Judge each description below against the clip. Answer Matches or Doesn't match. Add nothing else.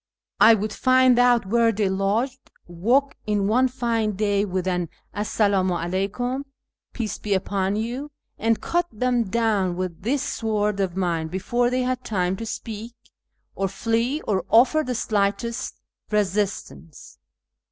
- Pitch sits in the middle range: Doesn't match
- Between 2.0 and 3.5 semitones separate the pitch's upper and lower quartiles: Doesn't match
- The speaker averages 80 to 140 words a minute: Doesn't match